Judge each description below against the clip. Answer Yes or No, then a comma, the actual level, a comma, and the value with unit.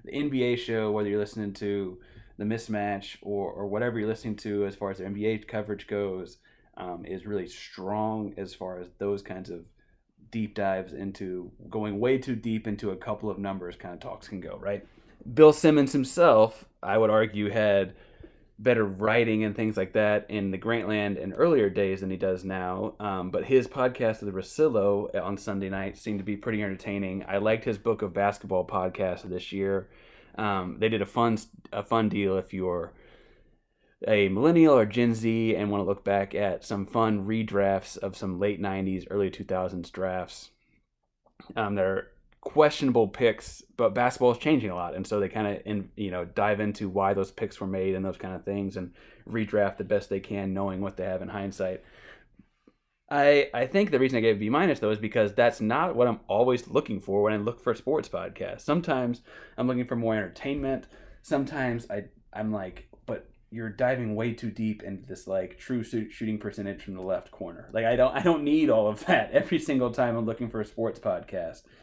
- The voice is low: Yes, low, 105 Hz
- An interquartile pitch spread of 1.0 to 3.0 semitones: Yes, average, 2.7 semitones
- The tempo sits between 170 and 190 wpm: No, average, 200 wpm